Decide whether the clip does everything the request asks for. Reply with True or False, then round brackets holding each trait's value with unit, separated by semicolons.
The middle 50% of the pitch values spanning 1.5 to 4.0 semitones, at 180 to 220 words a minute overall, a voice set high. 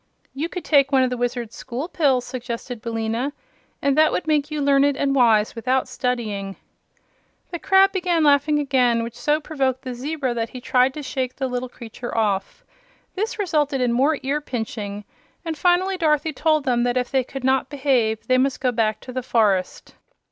True (3.6 semitones; 190 wpm; 260 Hz)